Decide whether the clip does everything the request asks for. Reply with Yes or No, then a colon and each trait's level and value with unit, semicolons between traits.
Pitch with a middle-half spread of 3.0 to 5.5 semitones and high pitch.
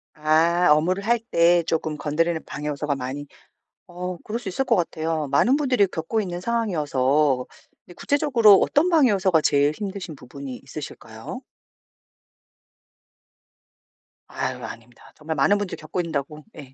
No: average, 5.2 semitones; medium, 165 Hz